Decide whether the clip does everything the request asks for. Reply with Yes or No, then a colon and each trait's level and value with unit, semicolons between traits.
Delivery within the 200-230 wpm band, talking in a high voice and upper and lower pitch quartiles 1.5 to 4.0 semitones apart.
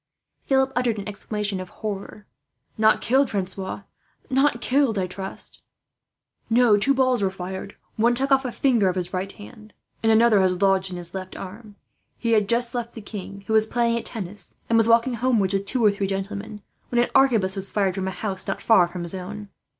Yes: fast, 205 wpm; high, 210 Hz; average, 3.6 semitones